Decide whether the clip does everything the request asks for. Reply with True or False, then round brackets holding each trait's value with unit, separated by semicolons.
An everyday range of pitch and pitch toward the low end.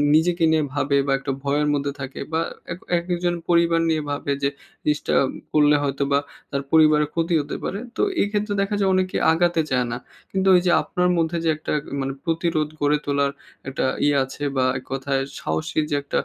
False (3.3 semitones; 155 Hz)